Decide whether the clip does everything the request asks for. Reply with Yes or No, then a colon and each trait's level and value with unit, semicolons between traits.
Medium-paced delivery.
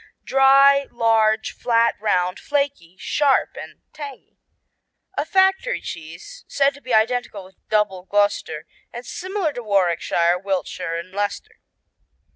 No: slow, 120 wpm